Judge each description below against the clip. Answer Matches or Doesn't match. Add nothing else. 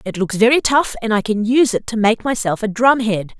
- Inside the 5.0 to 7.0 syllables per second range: Matches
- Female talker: Matches